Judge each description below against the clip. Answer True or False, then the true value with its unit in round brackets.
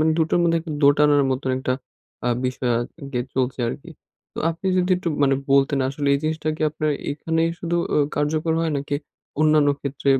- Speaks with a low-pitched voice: False (150 Hz)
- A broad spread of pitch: False (2.8 semitones)